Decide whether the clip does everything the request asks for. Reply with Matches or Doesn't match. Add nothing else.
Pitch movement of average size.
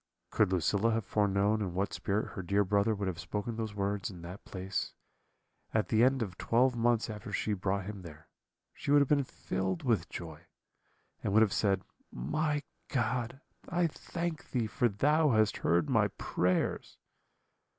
Matches